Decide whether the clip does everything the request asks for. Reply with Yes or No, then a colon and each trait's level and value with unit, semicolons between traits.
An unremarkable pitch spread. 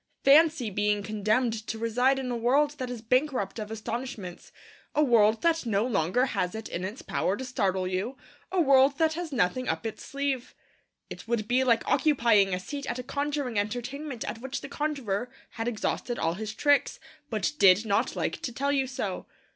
Yes: average, 4.4 semitones